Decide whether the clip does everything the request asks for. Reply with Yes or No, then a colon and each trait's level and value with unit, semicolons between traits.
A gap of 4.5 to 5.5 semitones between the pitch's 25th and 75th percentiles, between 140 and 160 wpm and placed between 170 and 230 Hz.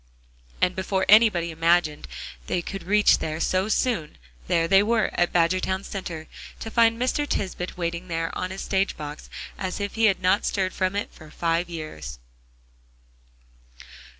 No: average, 3.2 semitones; average, 155 wpm; medium, 185 Hz